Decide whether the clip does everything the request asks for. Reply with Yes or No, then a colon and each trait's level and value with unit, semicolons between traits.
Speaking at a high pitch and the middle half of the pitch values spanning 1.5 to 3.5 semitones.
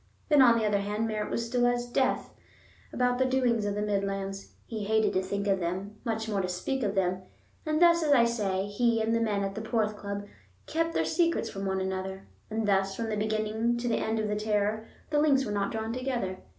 Yes: high, 215 Hz; average, 3.1 semitones